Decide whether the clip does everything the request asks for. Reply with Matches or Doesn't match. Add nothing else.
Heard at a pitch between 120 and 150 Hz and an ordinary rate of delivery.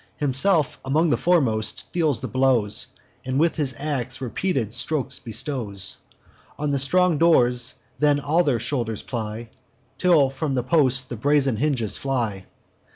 Matches